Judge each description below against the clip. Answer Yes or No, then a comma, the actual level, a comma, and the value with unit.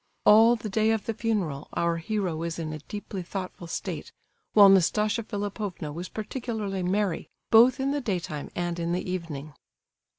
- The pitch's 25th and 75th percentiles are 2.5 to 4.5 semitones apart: Yes, average, 4.2 semitones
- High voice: Yes, high, 195 Hz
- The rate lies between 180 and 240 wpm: No, average, 165 wpm